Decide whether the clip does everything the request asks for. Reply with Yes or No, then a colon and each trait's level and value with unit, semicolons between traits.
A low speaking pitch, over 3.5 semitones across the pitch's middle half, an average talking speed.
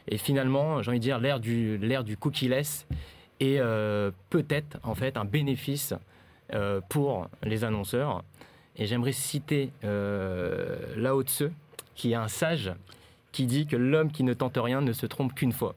Yes: low, 130 Hz; average, 4.4 semitones; average, 175 wpm